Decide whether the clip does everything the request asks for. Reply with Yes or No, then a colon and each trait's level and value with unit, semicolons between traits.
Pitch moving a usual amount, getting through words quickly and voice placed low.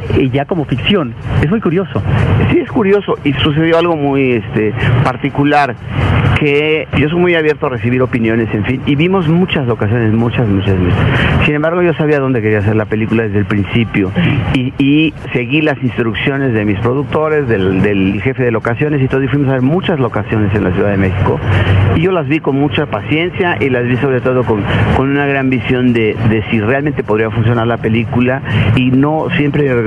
Yes: average, 4.7 semitones; fast, 195 wpm; low, 125 Hz